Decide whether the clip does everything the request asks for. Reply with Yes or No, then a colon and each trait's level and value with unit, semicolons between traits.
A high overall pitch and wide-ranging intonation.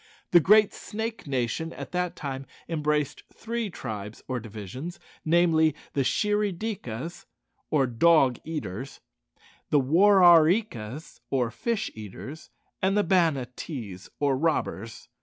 No: medium, 155 Hz; wide, 5.9 semitones